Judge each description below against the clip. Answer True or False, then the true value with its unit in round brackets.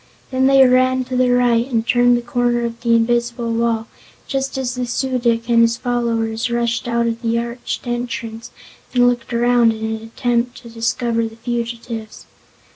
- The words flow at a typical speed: True (180 wpm)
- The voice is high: True (235 Hz)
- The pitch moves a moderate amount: False (1.1 semitones)